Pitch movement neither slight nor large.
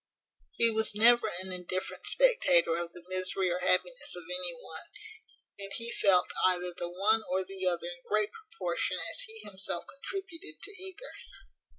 Yes: average, 5.0 semitones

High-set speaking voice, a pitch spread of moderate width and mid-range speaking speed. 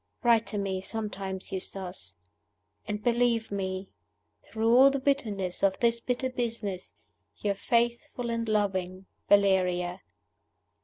No: high, 210 Hz; average, 3.7 semitones; slow, 115 wpm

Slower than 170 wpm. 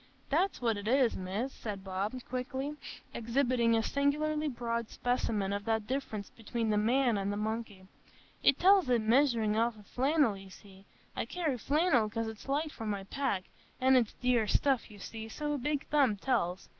No: average, 180 wpm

